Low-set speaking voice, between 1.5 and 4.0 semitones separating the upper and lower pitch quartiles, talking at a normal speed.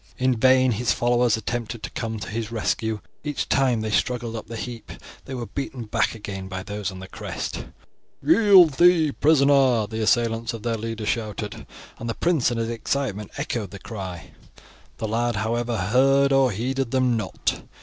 Yes: low, 115 Hz; average, 3.0 semitones; average, 180 wpm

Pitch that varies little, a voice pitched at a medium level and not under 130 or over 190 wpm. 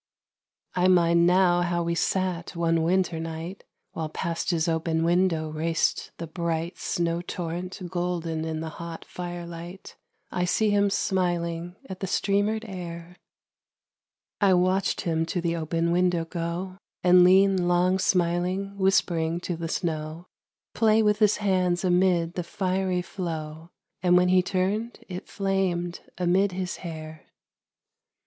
Yes: narrow, 1.8 semitones; medium, 175 Hz; average, 140 wpm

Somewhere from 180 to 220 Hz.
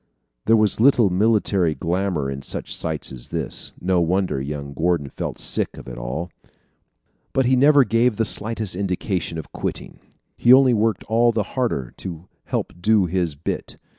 No: very low, 95 Hz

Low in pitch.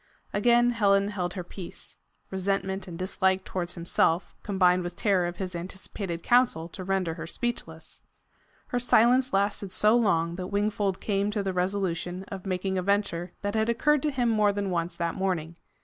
No: high, 190 Hz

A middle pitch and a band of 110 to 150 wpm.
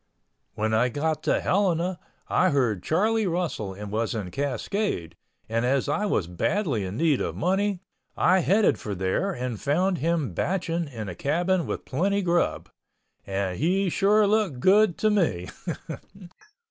Yes: medium, 160 Hz; average, 145 wpm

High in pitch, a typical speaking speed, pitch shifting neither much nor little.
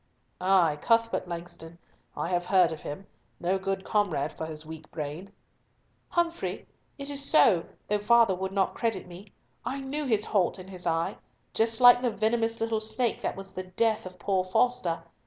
Yes: high, 195 Hz; average, 175 wpm; average, 4.6 semitones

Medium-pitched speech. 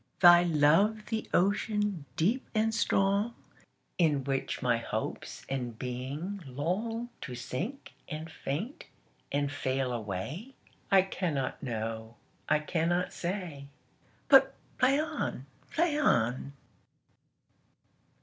Yes: medium, 165 Hz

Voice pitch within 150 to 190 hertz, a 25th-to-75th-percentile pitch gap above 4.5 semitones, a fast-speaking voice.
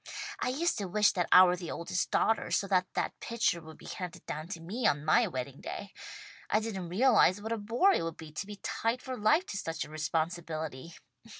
Yes: medium, 185 Hz; average, 5.2 semitones; fast, 220 wpm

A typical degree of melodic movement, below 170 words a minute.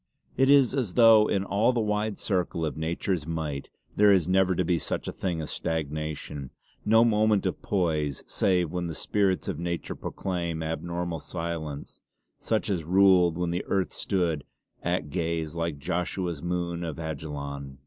Yes: average, 3.5 semitones; average, 160 wpm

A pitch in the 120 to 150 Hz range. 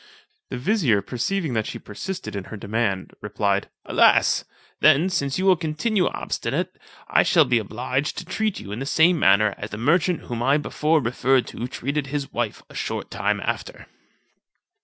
Yes: low, 135 Hz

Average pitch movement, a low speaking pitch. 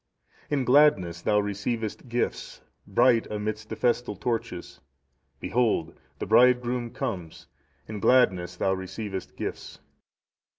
Yes: average, 4.3 semitones; low, 110 Hz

